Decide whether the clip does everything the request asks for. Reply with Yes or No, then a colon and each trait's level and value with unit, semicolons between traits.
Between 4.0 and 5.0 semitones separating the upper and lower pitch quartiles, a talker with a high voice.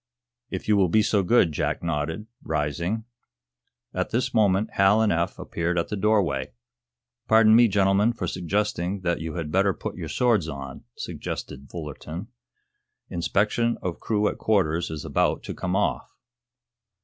No: average, 4.4 semitones; very low, 95 Hz